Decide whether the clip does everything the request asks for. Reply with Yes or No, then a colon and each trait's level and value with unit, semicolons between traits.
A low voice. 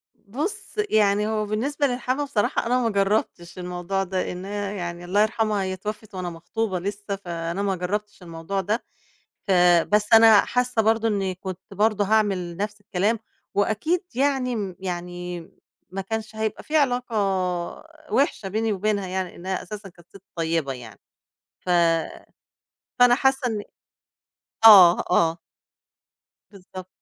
No: high, 205 Hz